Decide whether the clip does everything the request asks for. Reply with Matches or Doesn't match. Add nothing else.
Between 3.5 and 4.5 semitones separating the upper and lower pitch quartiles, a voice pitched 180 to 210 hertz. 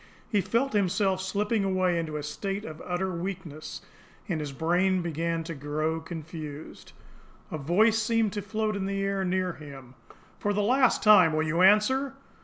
Matches